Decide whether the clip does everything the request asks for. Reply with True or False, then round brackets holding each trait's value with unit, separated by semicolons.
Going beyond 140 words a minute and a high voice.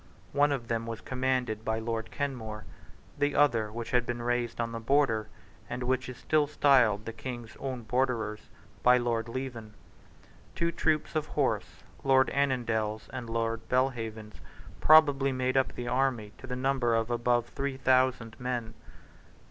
False (155 wpm; 120 Hz)